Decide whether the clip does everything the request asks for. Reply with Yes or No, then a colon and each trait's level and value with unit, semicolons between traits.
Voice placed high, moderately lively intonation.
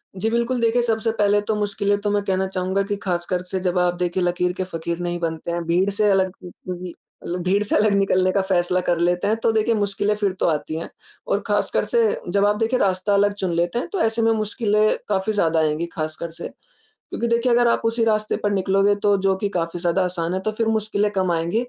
Yes: high, 195 Hz; average, 3.2 semitones